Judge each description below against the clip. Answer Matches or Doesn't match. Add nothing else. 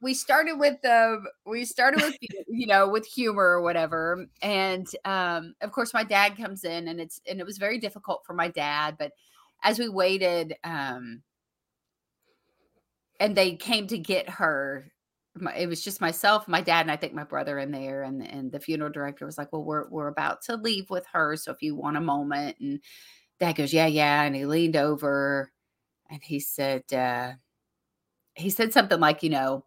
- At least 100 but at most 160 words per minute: Doesn't match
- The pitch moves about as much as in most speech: Doesn't match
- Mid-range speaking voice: Matches